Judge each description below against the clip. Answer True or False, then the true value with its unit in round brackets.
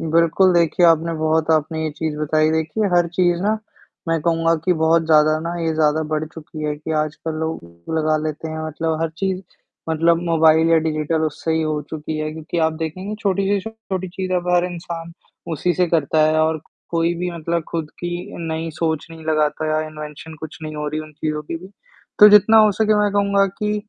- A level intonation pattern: True (2.1 semitones)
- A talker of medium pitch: True (160 Hz)